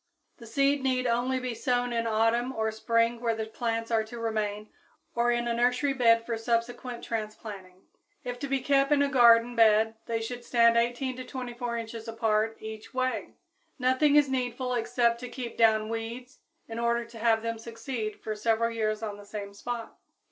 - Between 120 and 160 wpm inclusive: No, average, 185 wpm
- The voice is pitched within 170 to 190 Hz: No, high, 235 Hz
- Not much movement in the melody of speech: Yes, narrow, 1.7 semitones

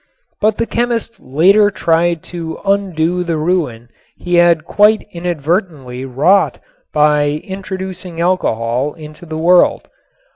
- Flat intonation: No, average, 3.8 semitones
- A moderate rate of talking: No, slow, 115 wpm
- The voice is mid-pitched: Yes, medium, 170 Hz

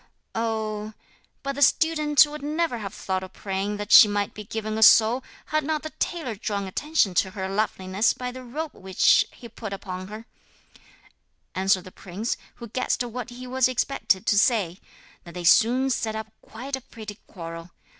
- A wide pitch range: No, average, 4.6 semitones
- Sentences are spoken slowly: No, average, 180 wpm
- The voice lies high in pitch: Yes, high, 220 Hz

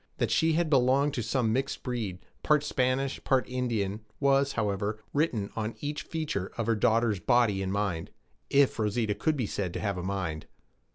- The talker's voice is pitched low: Yes, low, 115 Hz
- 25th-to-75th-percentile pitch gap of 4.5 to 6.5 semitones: Yes, average, 5.1 semitones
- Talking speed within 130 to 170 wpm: No, average, 180 wpm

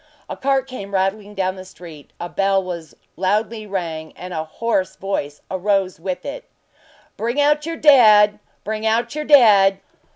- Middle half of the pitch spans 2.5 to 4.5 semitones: Yes, average, 3.9 semitones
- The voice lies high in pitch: Yes, high, 200 Hz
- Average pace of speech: Yes, average, 160 wpm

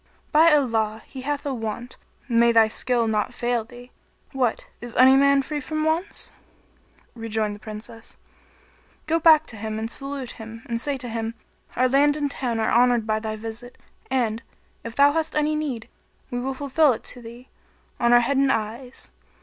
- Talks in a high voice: Yes, high, 245 Hz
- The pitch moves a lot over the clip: No, average, 3.7 semitones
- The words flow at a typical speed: Yes, average, 180 wpm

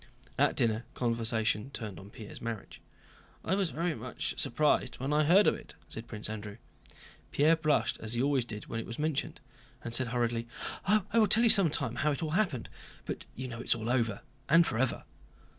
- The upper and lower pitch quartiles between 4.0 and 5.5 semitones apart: Yes, average, 5.2 semitones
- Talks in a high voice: No, low, 125 Hz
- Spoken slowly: No, average, 200 wpm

